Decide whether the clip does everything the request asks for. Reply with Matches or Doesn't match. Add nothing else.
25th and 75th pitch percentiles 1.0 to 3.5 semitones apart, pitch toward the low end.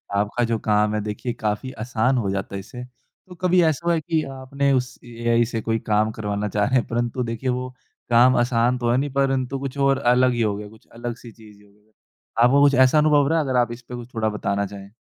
Matches